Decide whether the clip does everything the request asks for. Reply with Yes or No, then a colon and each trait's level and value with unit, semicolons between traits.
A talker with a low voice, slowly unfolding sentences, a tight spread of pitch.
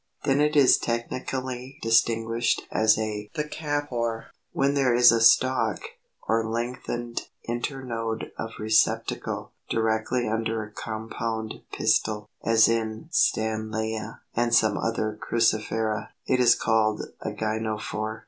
Yes: low, 115 Hz; slow, 115 wpm; narrow, 1.7 semitones